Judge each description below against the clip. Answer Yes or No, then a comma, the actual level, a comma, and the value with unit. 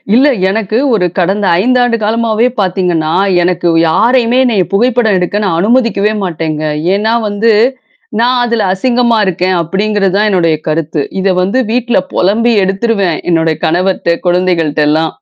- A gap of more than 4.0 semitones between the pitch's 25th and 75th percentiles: Yes, average, 4.7 semitones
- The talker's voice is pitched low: No, high, 195 Hz